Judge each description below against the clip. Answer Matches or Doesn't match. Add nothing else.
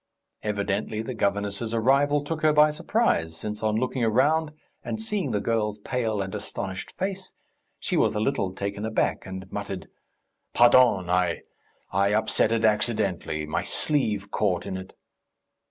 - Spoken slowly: Doesn't match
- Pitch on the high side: Doesn't match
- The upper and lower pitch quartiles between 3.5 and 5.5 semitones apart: Matches